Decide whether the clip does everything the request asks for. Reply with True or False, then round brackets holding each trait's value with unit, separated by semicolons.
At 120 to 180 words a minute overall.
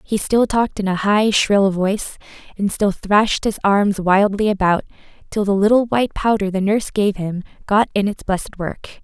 False (195 wpm)